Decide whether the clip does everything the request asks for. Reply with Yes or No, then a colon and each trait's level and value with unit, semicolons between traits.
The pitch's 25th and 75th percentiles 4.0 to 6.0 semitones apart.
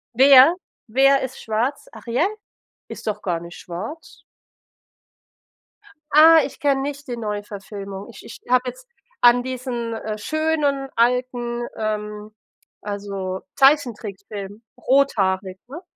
Yes: average, 4.8 semitones